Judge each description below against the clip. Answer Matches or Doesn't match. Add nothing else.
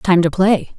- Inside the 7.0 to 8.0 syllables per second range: Doesn't match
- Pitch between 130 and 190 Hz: Matches